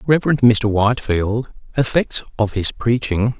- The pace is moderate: No, slow, 125 wpm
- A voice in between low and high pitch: No, low, 115 Hz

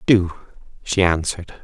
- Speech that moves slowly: Yes, slow, 110 wpm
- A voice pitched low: Yes, very low, 90 Hz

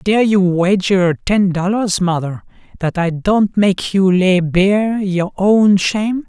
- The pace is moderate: Yes, average, 155 wpm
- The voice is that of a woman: No, male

